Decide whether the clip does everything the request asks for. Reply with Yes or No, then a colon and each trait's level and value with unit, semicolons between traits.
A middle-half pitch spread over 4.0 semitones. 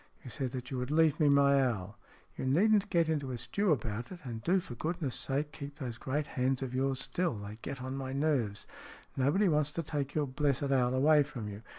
No: average, 3.3 semitones